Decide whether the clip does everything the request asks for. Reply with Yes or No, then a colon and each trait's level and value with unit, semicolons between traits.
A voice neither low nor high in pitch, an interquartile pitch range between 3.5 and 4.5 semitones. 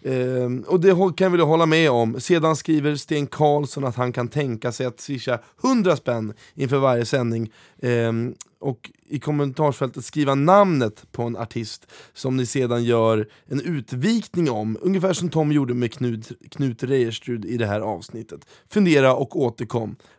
No: low, 130 Hz; average, 4.2 semitones